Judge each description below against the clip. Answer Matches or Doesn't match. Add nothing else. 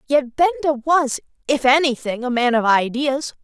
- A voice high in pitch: Matches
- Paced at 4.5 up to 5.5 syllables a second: Matches